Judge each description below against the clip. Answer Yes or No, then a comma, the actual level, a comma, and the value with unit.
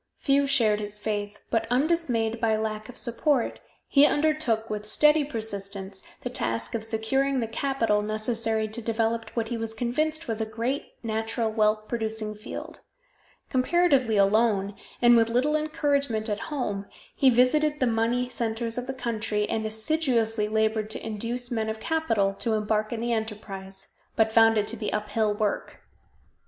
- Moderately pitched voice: No, high, 225 Hz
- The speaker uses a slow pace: No, average, 160 wpm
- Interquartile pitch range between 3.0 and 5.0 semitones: No, narrow, 2.6 semitones